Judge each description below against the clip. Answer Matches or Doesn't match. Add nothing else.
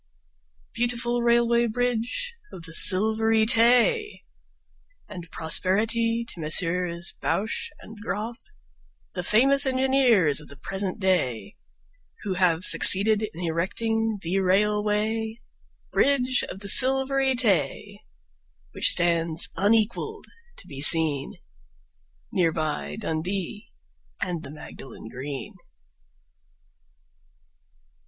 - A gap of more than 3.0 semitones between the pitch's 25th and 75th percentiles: Matches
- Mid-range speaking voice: Doesn't match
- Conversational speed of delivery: Doesn't match